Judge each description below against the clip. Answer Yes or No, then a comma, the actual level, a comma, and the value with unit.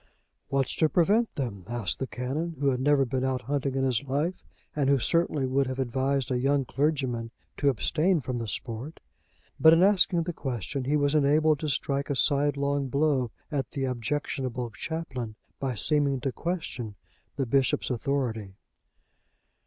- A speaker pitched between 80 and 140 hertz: Yes, low, 135 Hz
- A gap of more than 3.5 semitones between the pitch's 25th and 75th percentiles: No, average, 2.7 semitones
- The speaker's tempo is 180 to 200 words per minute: No, average, 165 wpm